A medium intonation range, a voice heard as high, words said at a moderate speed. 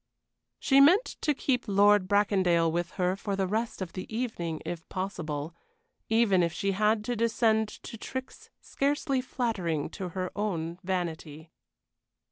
Yes: average, 4.6 semitones; high, 195 Hz; average, 145 wpm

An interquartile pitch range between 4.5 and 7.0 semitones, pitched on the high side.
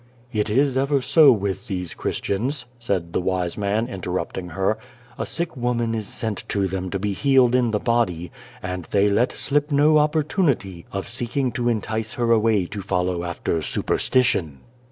No: average, 4.9 semitones; low, 110 Hz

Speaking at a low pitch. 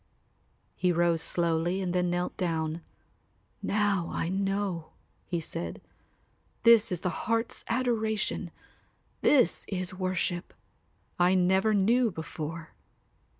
No: medium, 180 Hz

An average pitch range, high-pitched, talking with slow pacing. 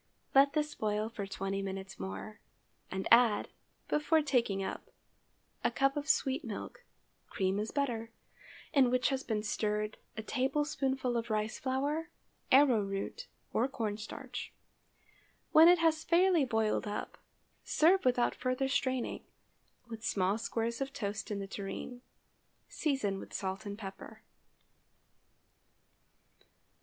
Yes: average, 4.9 semitones; high, 235 Hz; slow, 130 wpm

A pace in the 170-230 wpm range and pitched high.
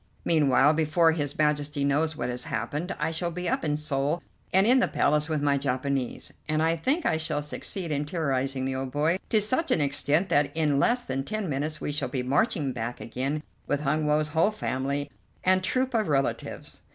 No: average, 200 wpm; medium, 150 Hz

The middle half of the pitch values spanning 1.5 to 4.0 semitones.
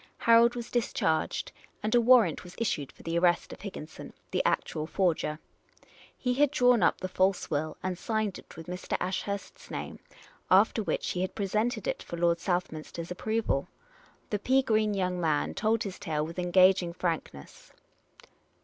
No: average, 4.4 semitones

